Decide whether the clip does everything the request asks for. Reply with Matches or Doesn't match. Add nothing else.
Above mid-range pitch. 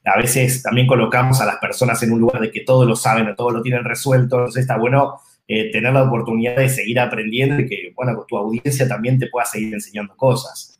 Doesn't match